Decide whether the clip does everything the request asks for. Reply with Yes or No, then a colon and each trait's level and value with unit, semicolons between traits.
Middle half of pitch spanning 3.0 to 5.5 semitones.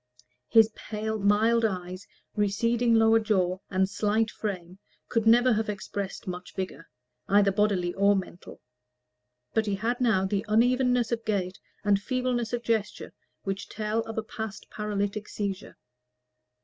No: narrow, 2.4 semitones